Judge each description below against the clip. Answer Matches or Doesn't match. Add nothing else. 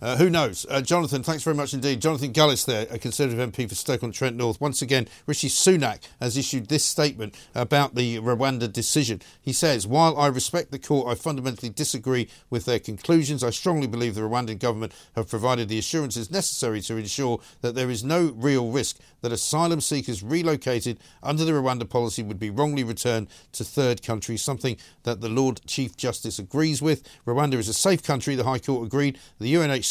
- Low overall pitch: Matches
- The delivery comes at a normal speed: Matches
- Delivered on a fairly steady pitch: Doesn't match